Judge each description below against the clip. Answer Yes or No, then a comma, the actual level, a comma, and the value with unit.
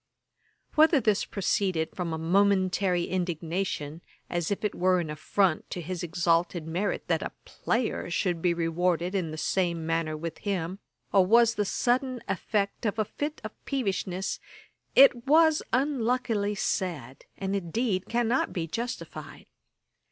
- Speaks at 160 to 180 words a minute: No, average, 145 wpm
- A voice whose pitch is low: No, high, 190 Hz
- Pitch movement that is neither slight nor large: Yes, average, 4.6 semitones